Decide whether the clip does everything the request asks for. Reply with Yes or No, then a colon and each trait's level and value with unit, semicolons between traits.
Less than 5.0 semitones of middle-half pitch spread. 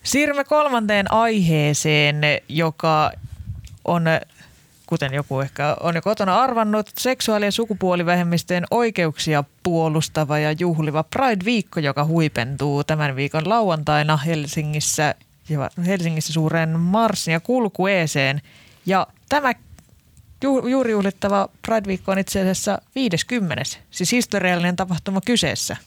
No: wide, 5.4 semitones